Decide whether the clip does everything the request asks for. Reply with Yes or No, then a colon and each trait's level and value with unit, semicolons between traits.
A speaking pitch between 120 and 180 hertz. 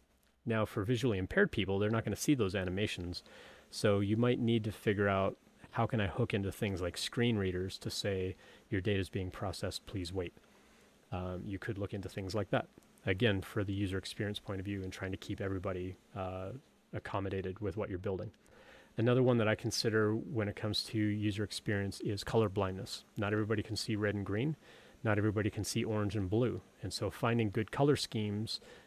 No: low, 105 Hz